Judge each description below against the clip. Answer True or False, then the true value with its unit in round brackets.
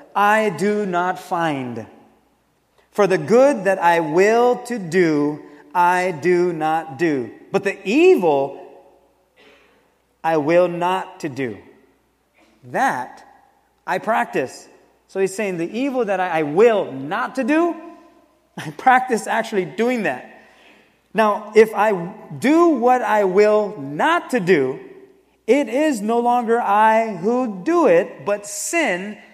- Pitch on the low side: False (210 Hz)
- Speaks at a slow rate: True (130 wpm)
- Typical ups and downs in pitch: False (5.9 semitones)